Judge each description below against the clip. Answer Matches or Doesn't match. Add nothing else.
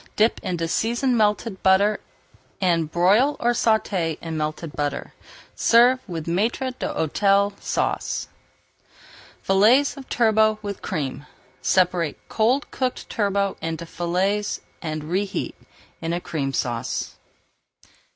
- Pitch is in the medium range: Doesn't match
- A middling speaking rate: Doesn't match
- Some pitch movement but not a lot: Matches